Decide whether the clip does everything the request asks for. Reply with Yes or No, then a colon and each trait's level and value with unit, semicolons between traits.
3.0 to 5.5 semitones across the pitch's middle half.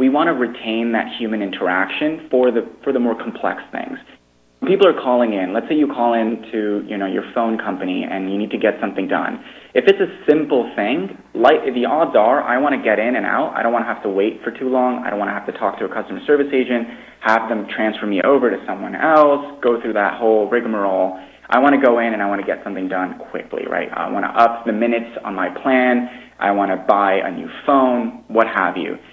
Yes: average, 3.4 semitones